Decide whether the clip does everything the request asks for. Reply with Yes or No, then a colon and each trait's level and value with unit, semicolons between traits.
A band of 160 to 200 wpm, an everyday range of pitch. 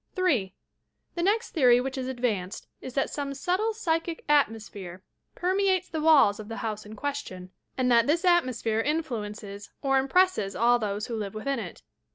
No: average, 170 wpm; wide, 7.0 semitones